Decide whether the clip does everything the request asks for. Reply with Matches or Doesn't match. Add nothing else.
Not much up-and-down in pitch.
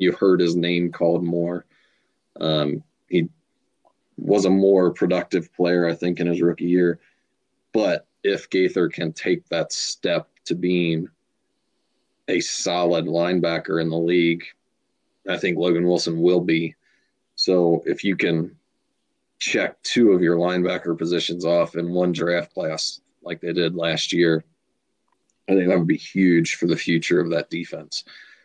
Matches